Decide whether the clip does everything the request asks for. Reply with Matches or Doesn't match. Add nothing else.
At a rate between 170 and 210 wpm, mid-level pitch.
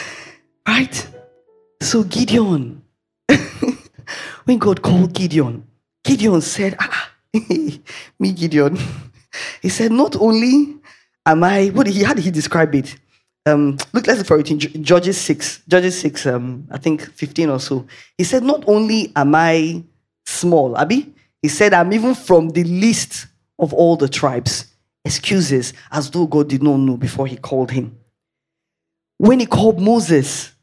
Doesn't match